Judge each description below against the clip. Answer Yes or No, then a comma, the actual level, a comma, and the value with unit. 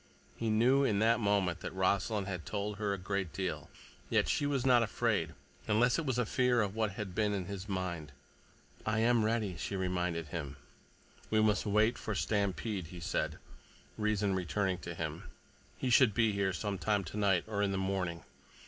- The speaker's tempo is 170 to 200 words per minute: Yes, average, 180 wpm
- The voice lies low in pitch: Yes, low, 100 Hz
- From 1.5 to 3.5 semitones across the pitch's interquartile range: Yes, average, 2.8 semitones